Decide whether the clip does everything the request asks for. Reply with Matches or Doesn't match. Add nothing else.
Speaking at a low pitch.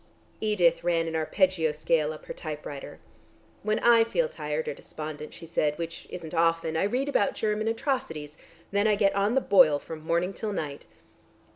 Doesn't match